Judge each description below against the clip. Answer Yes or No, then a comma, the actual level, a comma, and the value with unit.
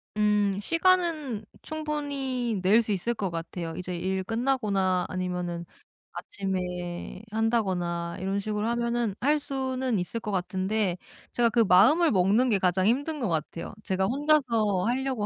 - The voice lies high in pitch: Yes, high, 210 Hz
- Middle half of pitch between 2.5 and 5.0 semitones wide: No, wide, 5.5 semitones